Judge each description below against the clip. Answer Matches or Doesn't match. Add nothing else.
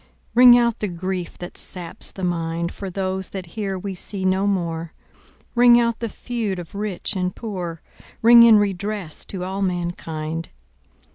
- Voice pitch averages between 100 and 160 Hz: Doesn't match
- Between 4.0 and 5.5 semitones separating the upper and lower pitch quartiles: Doesn't match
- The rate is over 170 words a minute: Doesn't match